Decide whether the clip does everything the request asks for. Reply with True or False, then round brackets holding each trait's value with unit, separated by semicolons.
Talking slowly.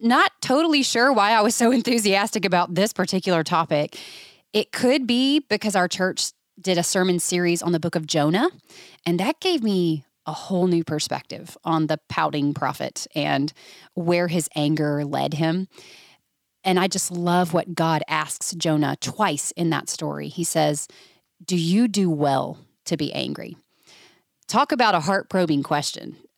False (165 wpm)